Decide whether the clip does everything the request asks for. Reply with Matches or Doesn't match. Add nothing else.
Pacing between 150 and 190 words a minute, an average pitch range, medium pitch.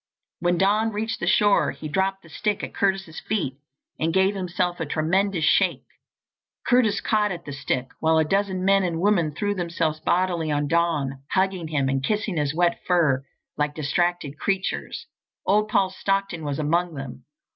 Matches